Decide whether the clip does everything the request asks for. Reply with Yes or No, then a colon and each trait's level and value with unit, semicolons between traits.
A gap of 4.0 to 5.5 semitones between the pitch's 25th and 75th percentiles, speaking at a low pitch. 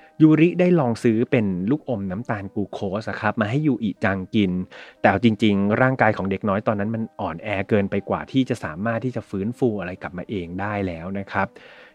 No: average, 3.6 semitones; low, 105 Hz